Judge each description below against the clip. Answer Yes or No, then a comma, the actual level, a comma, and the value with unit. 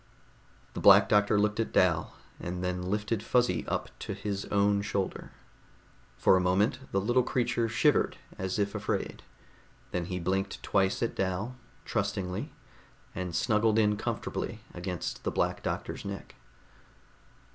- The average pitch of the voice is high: No, low, 100 Hz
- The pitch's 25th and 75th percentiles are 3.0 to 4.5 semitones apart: No, narrow, 2.5 semitones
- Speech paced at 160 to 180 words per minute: No, average, 140 wpm